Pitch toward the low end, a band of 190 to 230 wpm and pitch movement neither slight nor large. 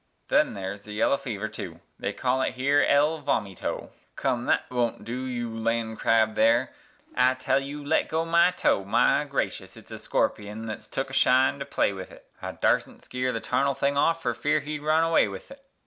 Yes: low, 125 Hz; average, 200 wpm; average, 4.3 semitones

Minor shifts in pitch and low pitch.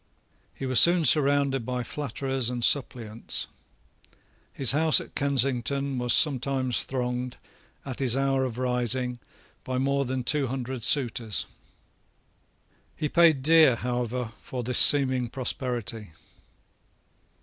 Yes: narrow, 2.1 semitones; low, 130 Hz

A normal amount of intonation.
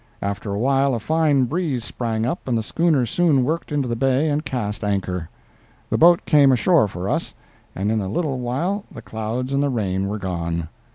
No: wide, 5.9 semitones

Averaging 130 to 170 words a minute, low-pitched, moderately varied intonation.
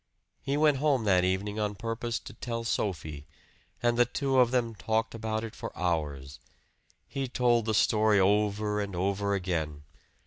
Yes: average, 165 wpm; low, 105 Hz; average, 3.9 semitones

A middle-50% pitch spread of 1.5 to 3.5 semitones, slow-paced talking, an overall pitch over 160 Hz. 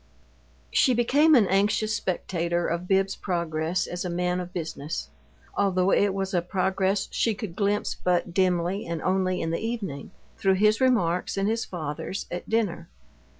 No: average, 2.9 semitones; average, 160 wpm; medium, 185 Hz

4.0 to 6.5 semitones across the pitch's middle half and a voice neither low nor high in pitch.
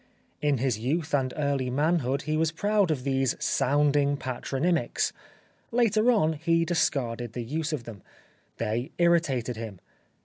Yes: average, 4.5 semitones; medium, 145 Hz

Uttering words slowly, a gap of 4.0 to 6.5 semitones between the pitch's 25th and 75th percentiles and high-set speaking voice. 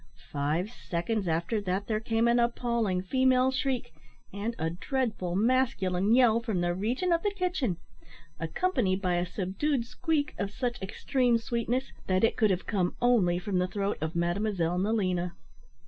No: average, 160 wpm; average, 5.2 semitones; high, 210 Hz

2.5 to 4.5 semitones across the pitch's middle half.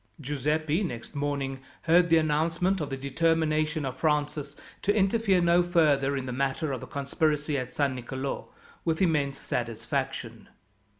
Yes: average, 3.1 semitones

